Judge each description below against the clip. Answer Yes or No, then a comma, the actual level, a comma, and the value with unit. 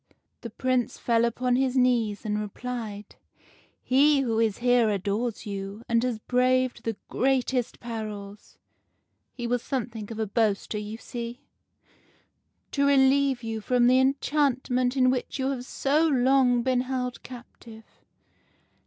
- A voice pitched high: Yes, high, 245 Hz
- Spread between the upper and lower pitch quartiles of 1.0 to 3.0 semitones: Yes, narrow, 2.5 semitones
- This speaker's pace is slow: No, average, 150 wpm